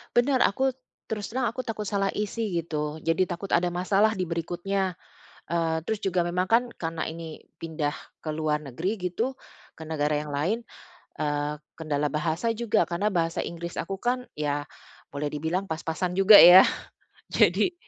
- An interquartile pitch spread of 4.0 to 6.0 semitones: Yes, average, 4.5 semitones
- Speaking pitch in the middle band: Yes, medium, 175 Hz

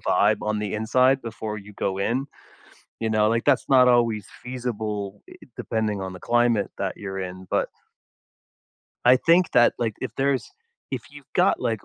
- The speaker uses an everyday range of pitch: Yes, average, 3.3 semitones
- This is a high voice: No, low, 110 Hz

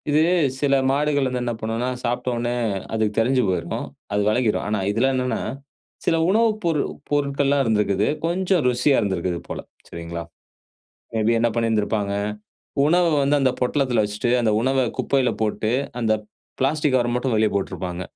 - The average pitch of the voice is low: Yes, low, 120 Hz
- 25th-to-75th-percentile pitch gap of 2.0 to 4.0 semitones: No, average, 4.4 semitones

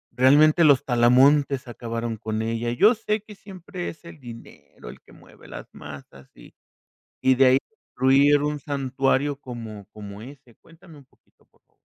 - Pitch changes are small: No, average, 3.9 semitones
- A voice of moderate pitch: No, low, 130 Hz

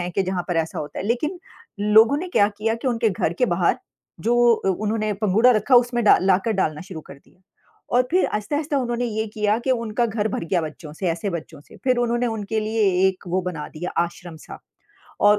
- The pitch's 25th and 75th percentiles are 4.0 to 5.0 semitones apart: Yes, average, 4.6 semitones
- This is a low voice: No, high, 215 Hz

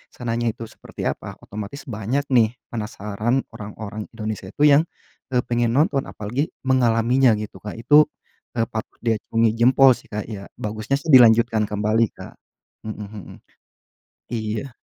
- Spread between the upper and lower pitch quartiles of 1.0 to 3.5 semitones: Yes, average, 2.9 semitones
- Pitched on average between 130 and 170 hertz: No, low, 115 Hz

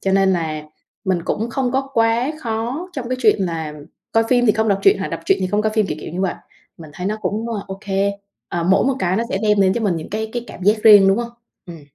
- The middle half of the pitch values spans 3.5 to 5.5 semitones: Yes, average, 3.8 semitones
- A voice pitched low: No, high, 210 Hz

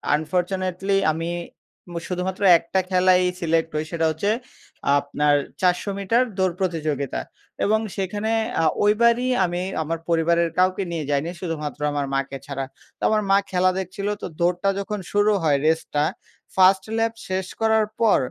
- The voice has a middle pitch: Yes, medium, 180 Hz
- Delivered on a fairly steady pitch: No, average, 3.4 semitones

